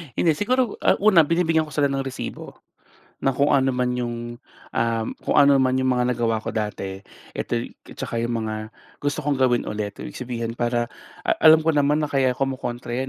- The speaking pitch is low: Yes, low, 130 Hz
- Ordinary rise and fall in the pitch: Yes, average, 3.5 semitones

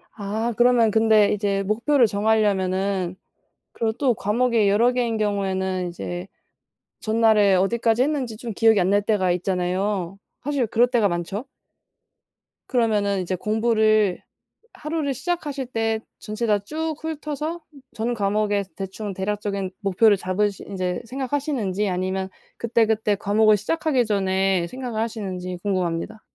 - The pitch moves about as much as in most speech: Yes, average, 3.4 semitones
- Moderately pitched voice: No, high, 210 Hz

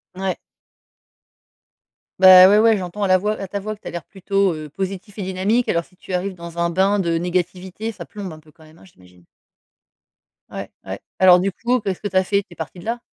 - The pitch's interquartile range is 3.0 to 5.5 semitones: No, narrow, 2.6 semitones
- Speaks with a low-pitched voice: No, medium, 185 Hz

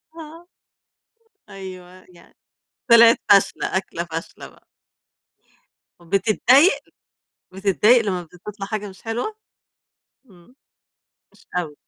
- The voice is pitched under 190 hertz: No, high, 195 Hz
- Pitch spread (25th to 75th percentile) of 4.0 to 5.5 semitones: Yes, average, 4.5 semitones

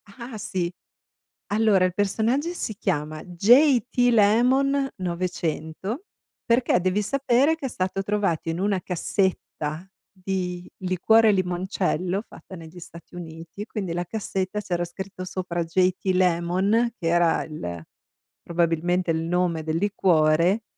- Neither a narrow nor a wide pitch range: Yes, average, 3.5 semitones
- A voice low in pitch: No, medium, 185 Hz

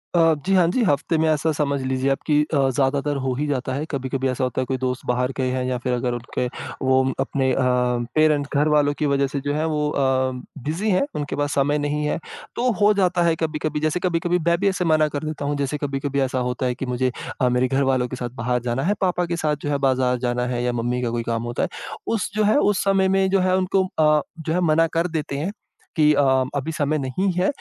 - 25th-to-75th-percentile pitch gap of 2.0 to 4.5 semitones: Yes, average, 3.7 semitones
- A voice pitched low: No, medium, 145 Hz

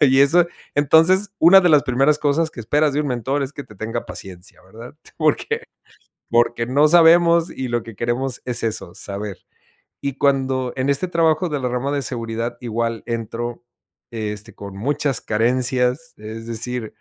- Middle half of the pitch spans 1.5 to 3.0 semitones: No, average, 4.2 semitones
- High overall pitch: No, low, 130 Hz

